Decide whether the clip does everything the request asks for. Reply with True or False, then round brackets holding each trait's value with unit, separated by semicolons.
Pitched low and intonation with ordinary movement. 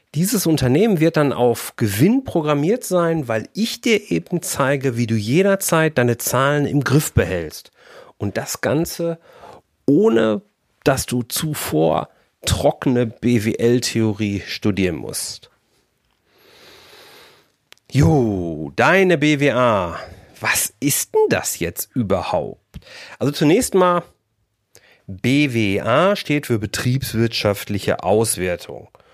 False (130 Hz; 6.6 semitones)